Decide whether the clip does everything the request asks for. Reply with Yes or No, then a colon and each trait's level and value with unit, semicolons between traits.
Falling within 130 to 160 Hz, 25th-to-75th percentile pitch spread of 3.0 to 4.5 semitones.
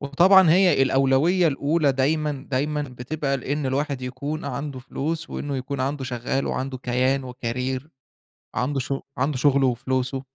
No: low, 135 Hz; narrow, 2.4 semitones